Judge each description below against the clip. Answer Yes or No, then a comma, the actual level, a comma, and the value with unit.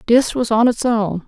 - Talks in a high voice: Yes, high, 230 Hz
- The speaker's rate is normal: No, fast, 235 wpm